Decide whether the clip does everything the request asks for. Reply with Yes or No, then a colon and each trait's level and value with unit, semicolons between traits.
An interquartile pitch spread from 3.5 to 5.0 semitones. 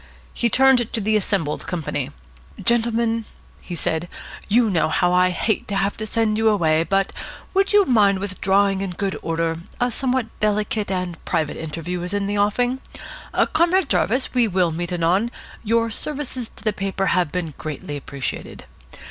Yes: average, 4.5 semitones